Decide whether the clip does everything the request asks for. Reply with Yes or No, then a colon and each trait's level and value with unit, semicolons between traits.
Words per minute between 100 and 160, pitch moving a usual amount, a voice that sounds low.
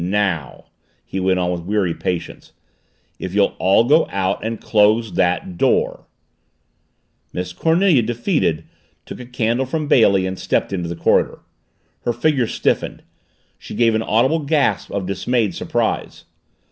Yes: average, 150 wpm; average, 4.8 semitones; low, 105 Hz